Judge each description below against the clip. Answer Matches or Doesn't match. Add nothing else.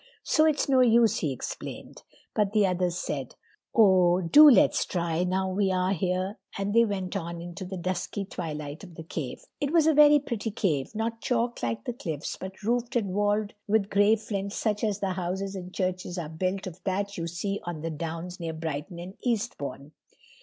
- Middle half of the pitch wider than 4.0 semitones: Doesn't match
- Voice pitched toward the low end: Doesn't match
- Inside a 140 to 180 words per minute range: Doesn't match